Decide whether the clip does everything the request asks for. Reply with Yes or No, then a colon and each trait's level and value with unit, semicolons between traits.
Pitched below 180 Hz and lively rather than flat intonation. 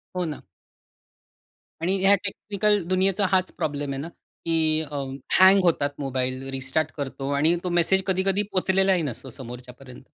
Yes: medium, 160 Hz; wide, 5.8 semitones